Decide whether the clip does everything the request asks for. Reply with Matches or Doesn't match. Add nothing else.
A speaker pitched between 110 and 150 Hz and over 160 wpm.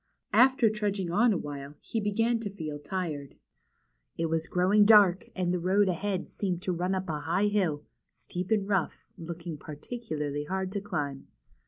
Doesn't match